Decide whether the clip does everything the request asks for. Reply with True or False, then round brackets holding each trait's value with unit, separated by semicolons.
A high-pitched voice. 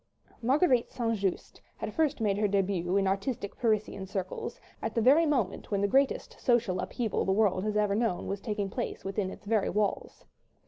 True (210 Hz)